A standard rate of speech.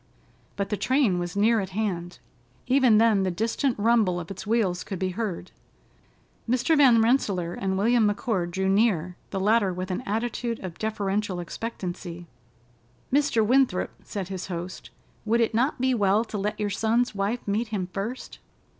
Yes: average, 165 wpm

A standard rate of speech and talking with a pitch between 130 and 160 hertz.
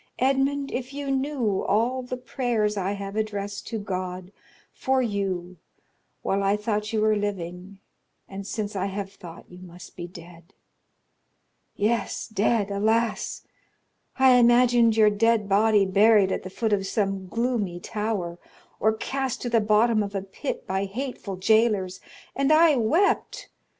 No: average, 150 wpm; high, 210 Hz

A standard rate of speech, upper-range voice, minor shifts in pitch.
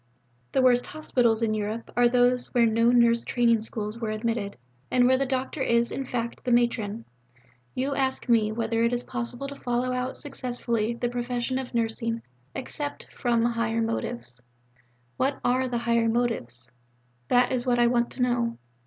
Yes: average, 170 wpm; high, 240 Hz; narrow, 1.5 semitones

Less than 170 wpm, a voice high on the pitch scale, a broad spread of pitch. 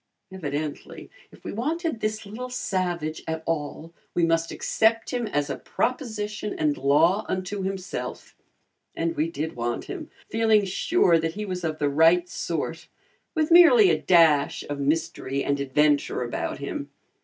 No: average, 155 wpm; medium, 170 Hz; wide, 5.9 semitones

